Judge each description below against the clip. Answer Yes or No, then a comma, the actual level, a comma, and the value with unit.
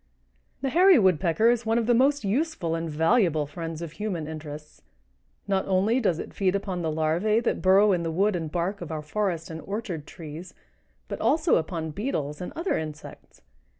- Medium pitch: Yes, medium, 180 Hz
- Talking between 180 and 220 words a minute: Yes, average, 185 wpm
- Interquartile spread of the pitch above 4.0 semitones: Yes, average, 5.1 semitones